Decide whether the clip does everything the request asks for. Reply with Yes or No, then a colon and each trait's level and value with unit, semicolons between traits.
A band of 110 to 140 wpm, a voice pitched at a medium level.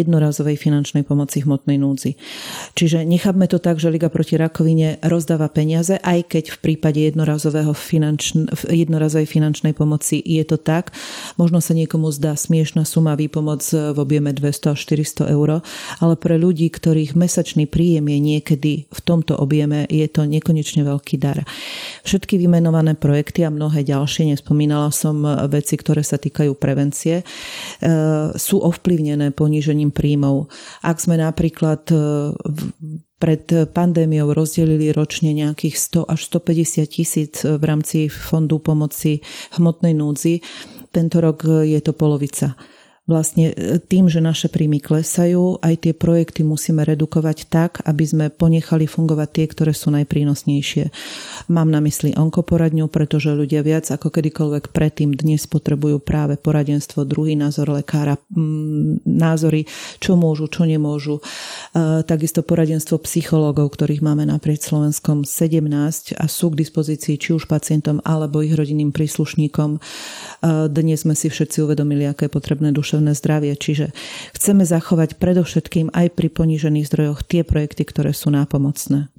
Yes: average, 135 wpm; medium, 155 Hz